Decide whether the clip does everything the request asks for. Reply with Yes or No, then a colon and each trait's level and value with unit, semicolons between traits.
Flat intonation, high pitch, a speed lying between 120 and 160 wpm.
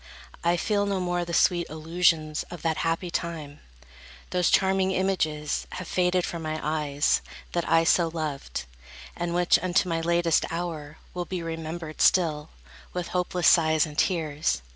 No: narrow, 2.2 semitones; medium, 170 Hz; average, 155 wpm